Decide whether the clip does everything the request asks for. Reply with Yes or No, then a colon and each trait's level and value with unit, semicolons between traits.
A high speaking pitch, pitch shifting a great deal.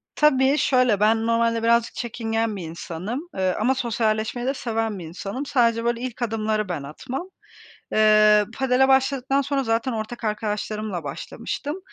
No: high, 230 Hz; average, 3.2 semitones